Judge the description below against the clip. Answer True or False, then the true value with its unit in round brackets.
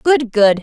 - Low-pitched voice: False (240 Hz)